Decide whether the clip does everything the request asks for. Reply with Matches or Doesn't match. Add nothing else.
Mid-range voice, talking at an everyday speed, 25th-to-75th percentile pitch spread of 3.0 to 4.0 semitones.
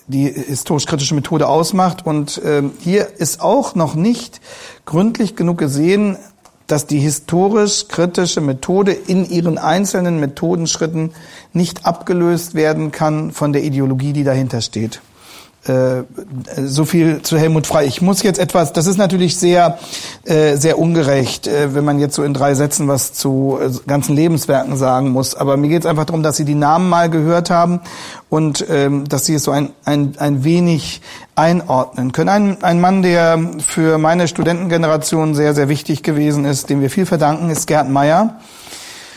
Matches